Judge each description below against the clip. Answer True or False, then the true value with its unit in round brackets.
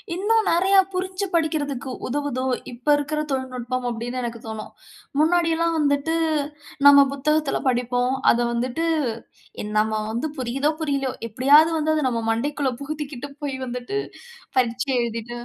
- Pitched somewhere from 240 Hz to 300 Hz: True (275 Hz)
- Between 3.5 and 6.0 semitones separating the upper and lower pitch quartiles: True (4.1 semitones)